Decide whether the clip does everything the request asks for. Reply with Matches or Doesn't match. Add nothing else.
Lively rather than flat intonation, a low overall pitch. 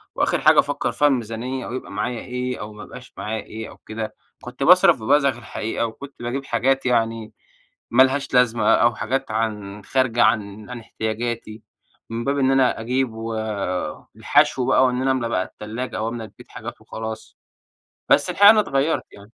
Doesn't match